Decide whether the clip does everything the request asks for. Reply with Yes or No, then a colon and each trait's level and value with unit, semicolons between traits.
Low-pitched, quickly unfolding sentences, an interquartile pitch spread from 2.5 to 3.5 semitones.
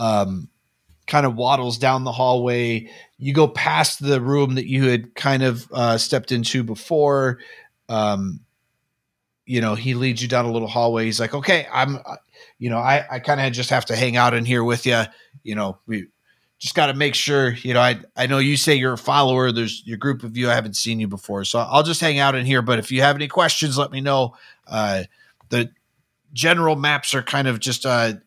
Yes: low, 125 Hz; fast, 220 wpm; average, 3.1 semitones